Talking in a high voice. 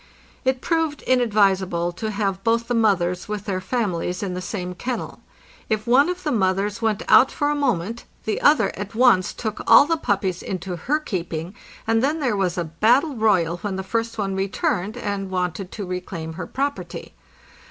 Yes: high, 205 Hz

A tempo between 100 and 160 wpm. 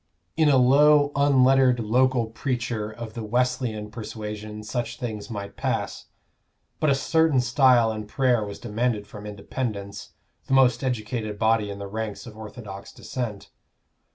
Yes: average, 145 wpm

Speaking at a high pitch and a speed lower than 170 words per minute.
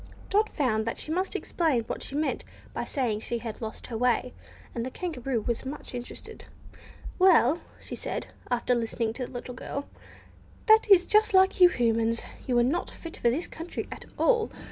No: very high, 255 Hz; average, 190 wpm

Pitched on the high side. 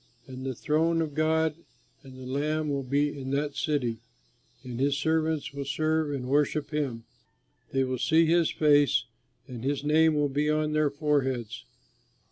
No: medium, 145 Hz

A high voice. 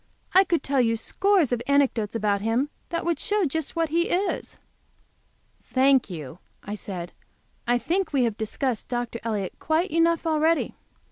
Yes: very high, 270 Hz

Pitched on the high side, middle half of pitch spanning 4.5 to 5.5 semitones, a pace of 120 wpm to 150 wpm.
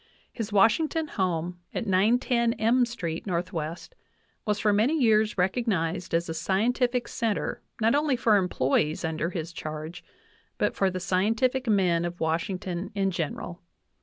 Yes: high, 195 Hz; average, 5.1 semitones; average, 145 wpm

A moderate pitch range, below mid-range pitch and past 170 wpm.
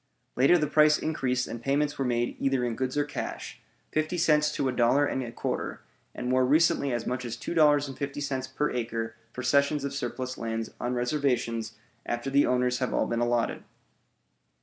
Yes: average, 3.2 semitones; low, 130 Hz; average, 180 wpm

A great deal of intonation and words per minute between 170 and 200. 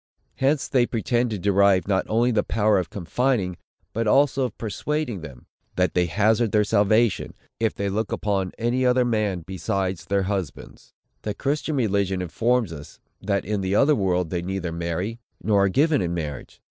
No: average, 4.2 semitones; average, 175 wpm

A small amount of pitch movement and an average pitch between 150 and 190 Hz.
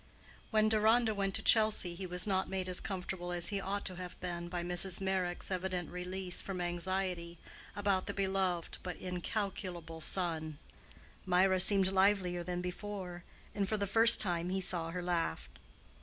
Yes: narrow, 1.8 semitones; medium, 185 Hz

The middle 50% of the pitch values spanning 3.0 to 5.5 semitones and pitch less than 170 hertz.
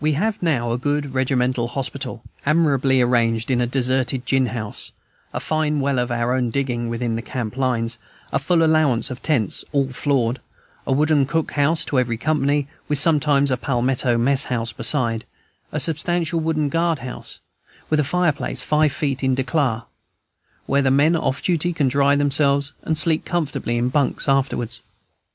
Yes: average, 3.4 semitones; low, 135 Hz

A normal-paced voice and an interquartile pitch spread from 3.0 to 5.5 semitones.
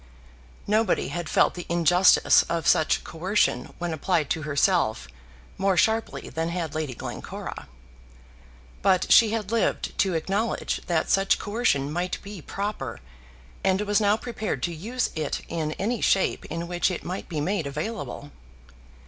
Yes: average, 150 wpm; average, 4.3 semitones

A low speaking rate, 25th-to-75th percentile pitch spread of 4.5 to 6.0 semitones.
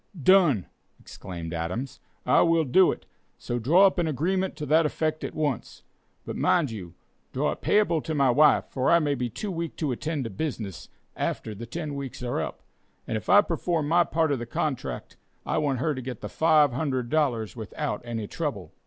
No: average, 195 wpm; average, 5.3 semitones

